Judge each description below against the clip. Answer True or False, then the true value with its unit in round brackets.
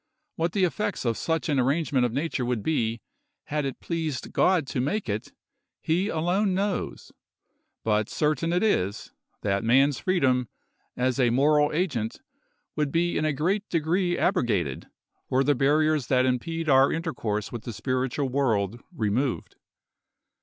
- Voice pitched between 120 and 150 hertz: True (140 Hz)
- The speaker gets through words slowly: False (150 wpm)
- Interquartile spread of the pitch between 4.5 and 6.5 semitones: True (5.1 semitones)